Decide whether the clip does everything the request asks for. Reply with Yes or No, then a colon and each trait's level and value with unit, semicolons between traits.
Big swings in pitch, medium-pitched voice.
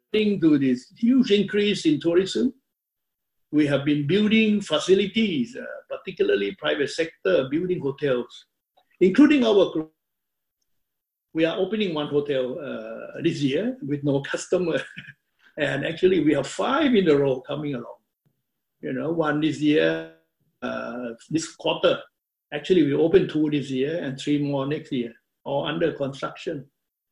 Yes: wide, 6.3 semitones; medium, 155 Hz